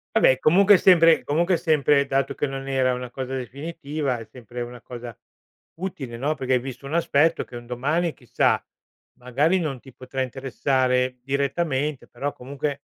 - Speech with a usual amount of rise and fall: Yes, average, 3.3 semitones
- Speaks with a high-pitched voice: No, low, 135 Hz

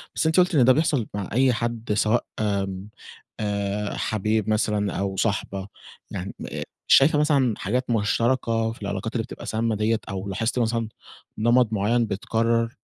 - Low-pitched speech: Yes, low, 110 Hz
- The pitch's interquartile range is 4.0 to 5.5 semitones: No, narrow, 2.6 semitones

